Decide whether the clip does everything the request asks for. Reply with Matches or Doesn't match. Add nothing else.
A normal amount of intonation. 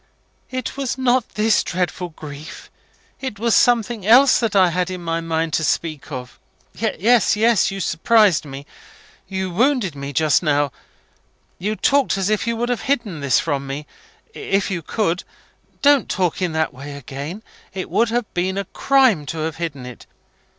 Doesn't match